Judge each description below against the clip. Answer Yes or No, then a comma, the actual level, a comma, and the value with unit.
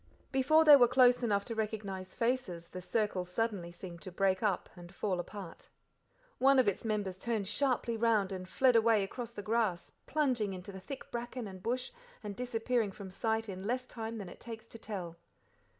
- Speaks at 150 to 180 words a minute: No, average, 190 wpm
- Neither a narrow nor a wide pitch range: Yes, average, 4.0 semitones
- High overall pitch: Yes, high, 215 Hz